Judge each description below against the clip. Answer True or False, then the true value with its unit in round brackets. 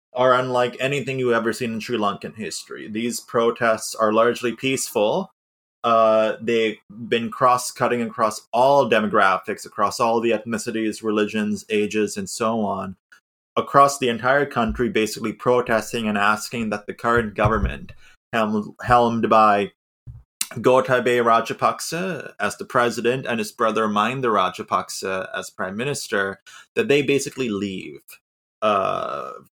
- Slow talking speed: True (130 wpm)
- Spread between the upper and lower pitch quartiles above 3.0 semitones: False (2.4 semitones)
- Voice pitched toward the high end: False (115 Hz)